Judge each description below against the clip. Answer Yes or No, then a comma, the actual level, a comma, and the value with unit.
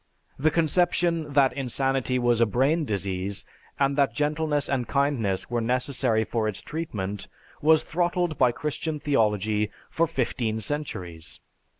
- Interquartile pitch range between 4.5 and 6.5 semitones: Yes, wide, 5.5 semitones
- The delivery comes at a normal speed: No, slow, 130 wpm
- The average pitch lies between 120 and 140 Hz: Yes, low, 135 Hz